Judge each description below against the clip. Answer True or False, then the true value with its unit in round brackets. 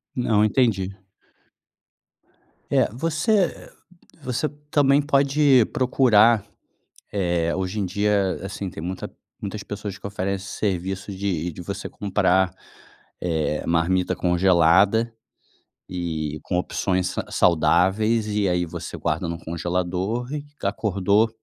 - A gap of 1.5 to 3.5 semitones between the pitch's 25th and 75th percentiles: False (3.9 semitones)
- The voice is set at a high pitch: False (95 Hz)